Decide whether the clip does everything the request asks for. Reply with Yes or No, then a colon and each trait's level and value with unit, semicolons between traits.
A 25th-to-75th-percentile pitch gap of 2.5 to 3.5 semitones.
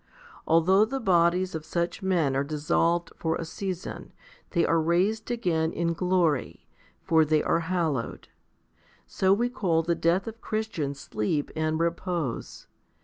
Yes: average, 2.8 semitones